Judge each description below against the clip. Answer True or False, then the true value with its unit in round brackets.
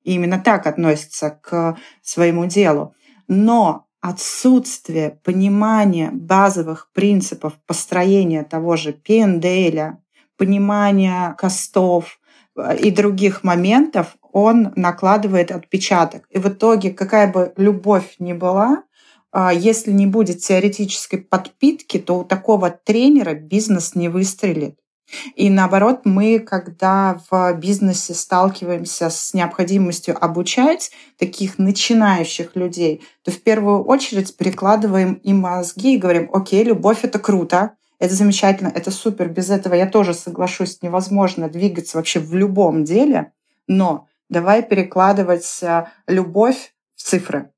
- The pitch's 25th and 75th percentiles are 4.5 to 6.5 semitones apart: False (2.7 semitones)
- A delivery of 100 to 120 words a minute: True (115 wpm)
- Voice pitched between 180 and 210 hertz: True (190 Hz)